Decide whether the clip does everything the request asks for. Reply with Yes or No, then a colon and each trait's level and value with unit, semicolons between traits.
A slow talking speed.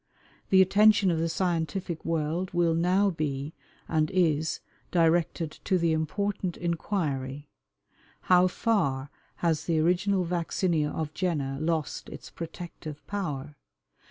Yes: slow, 120 wpm